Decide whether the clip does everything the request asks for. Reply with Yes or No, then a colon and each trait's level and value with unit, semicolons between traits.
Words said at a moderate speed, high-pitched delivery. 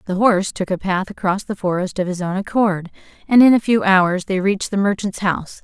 No: fast, 235 wpm; high, 195 Hz